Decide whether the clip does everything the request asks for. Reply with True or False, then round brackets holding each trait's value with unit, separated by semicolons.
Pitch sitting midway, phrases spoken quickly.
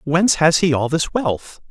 True (160 Hz; 210 wpm)